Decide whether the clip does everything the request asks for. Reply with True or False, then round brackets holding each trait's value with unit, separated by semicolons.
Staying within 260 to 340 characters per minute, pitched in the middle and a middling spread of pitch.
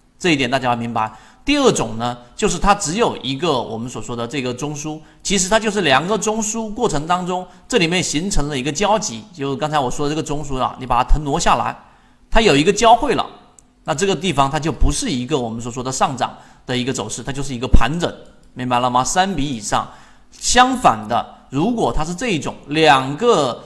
False (320 characters per minute; 150 Hz; 7.9 semitones)